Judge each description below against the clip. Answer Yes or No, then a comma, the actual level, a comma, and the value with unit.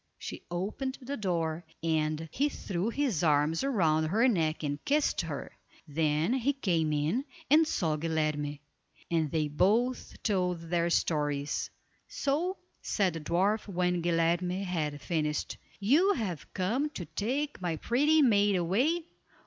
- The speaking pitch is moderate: Yes, medium, 180 Hz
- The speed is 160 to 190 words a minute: No, average, 140 wpm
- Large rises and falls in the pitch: Yes, wide, 7.2 semitones